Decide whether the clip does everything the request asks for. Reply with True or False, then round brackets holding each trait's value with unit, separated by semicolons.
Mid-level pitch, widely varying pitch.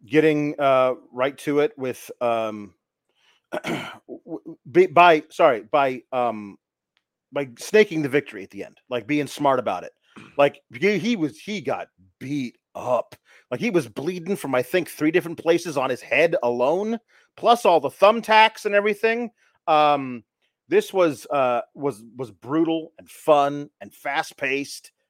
True (150 Hz; 5.7 semitones)